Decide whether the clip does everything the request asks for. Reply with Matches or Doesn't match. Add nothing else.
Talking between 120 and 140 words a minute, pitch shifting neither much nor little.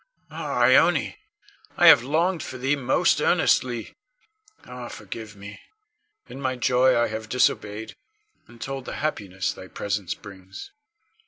Matches